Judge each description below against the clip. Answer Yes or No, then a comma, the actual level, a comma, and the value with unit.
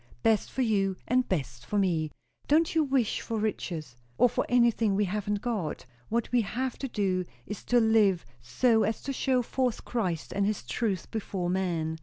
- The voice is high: Yes, high, 210 Hz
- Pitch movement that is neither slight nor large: Yes, average, 4.7 semitones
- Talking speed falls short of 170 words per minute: No, average, 185 wpm